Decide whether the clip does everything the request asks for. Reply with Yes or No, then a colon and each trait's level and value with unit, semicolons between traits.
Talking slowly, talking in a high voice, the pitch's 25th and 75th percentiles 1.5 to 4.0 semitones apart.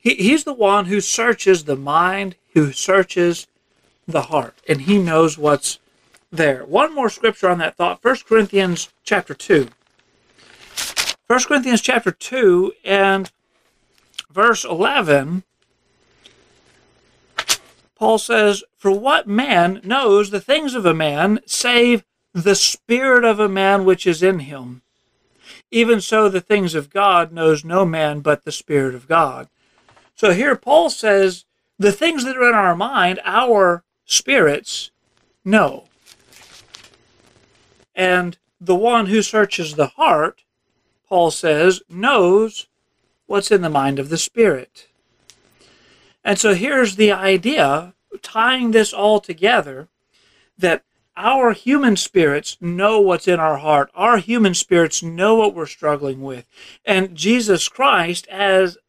No: slow, 130 wpm; high, 195 Hz; average, 4.8 semitones